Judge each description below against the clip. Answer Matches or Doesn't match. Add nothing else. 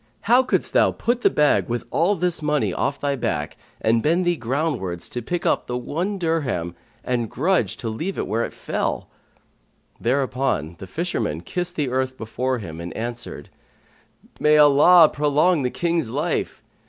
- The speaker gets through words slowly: Doesn't match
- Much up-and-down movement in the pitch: Matches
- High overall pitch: Doesn't match